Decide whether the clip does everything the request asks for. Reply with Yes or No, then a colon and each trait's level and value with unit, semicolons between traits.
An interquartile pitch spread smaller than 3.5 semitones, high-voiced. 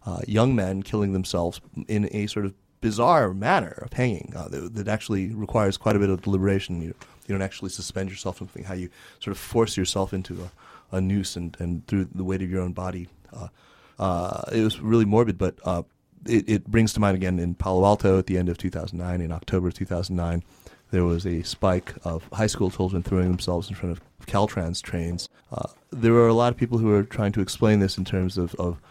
No: average, 2.7 semitones; very low, 95 Hz